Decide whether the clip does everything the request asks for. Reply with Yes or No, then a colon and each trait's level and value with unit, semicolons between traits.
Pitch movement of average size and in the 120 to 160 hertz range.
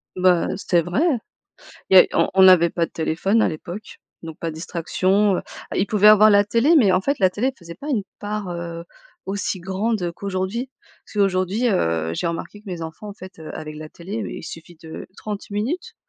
No: average, 3.7 semitones; high, 190 Hz